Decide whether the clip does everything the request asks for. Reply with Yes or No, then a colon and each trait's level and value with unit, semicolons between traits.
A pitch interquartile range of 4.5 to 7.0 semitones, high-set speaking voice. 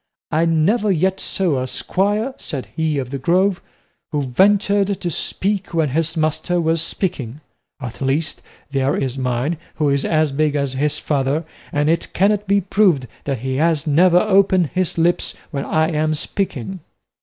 No: average, 4.9 semitones; medium, 160 Hz